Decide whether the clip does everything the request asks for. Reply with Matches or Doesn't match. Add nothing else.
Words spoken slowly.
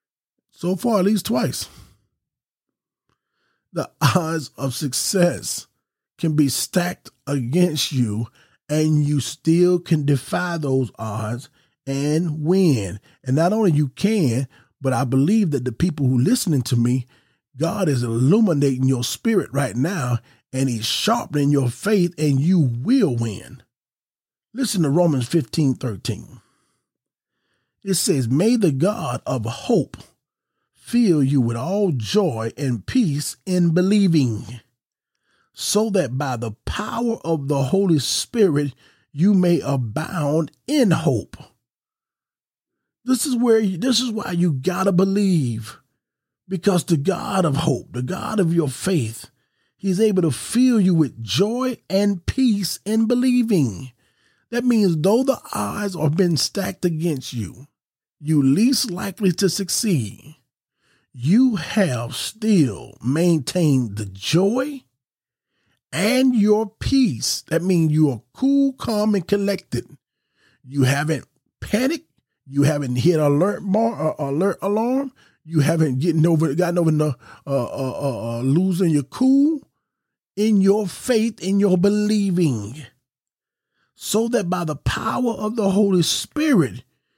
Matches